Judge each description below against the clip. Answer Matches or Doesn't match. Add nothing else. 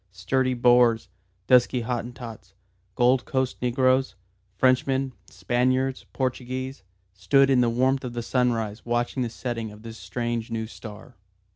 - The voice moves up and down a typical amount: Doesn't match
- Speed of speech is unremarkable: Doesn't match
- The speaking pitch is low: Matches